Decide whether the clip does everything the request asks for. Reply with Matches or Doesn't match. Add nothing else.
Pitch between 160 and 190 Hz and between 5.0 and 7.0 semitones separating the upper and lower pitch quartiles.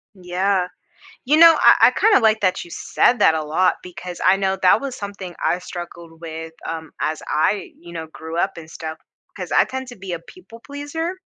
Matches